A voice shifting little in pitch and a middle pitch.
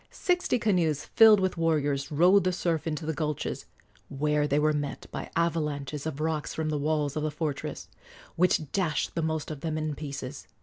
Yes: narrow, 2.1 semitones; medium, 155 Hz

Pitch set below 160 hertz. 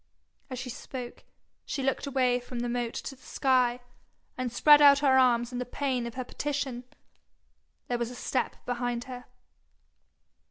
No: very high, 250 Hz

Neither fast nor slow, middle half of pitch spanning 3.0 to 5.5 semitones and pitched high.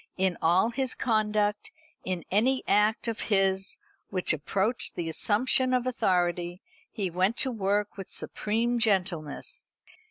No: slow, 130 wpm; average, 4.0 semitones; high, 205 Hz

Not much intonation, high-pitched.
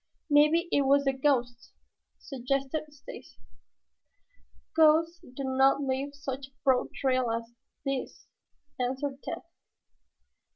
Yes: narrow, 1.8 semitones; very high, 270 Hz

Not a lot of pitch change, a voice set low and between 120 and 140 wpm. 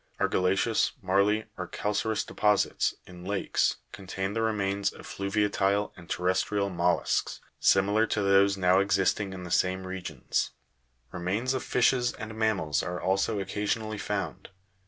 Yes: narrow, 2.1 semitones; low, 100 Hz; slow, 135 wpm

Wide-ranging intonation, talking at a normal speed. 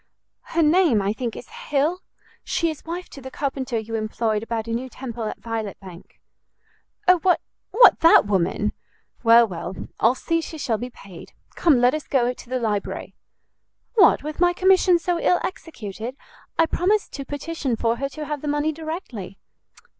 Yes: wide, 6.5 semitones; average, 175 wpm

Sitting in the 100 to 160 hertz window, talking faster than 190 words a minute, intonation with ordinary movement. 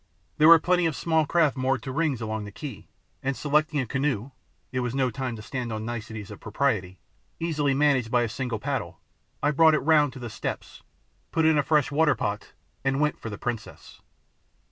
Yes: low, 135 Hz; fast, 205 wpm; average, 4.6 semitones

